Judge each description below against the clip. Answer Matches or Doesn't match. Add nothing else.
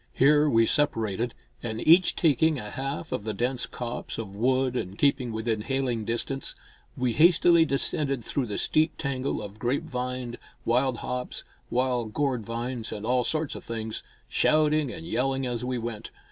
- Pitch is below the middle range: Matches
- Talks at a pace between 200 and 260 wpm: Doesn't match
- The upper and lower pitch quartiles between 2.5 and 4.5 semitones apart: Matches